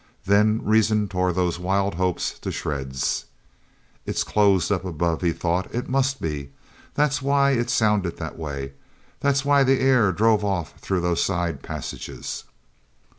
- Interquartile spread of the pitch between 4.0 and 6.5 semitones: Yes, wide, 5.5 semitones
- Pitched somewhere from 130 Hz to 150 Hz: No, low, 100 Hz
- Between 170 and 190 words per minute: No, average, 150 wpm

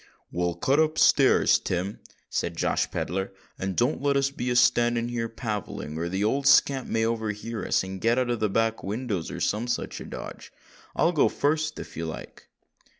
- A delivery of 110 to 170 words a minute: No, average, 190 wpm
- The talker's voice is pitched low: Yes, low, 115 Hz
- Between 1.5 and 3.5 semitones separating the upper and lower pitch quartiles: No, average, 5.0 semitones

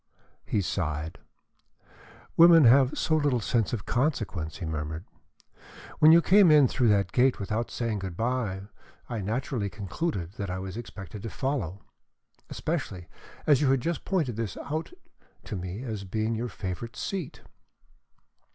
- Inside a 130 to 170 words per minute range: Yes, average, 150 wpm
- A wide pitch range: Yes, wide, 5.8 semitones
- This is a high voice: No, low, 115 Hz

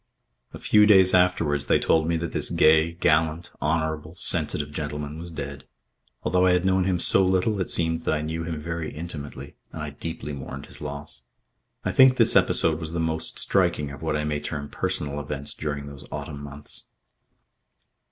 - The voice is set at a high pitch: No, very low, 80 Hz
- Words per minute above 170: Yes, average, 185 wpm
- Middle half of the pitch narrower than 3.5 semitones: Yes, narrow, 2.5 semitones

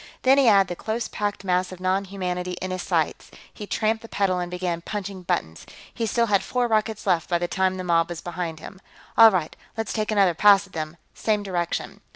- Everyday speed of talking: No, fast, 220 wpm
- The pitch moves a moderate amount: Yes, average, 3.0 semitones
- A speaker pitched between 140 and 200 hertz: Yes, high, 190 Hz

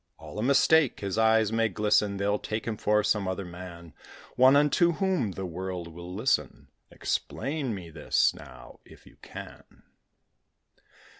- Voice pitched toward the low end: Yes, low, 105 Hz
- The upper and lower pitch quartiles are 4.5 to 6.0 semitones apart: Yes, average, 5.0 semitones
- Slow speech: No, average, 150 wpm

